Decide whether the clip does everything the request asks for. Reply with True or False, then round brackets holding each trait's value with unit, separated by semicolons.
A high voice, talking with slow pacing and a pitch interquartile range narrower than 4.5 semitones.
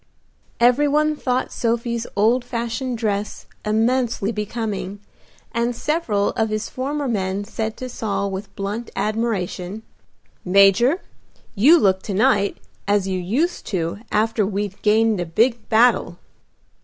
True (220 Hz; 130 wpm; 3.2 semitones)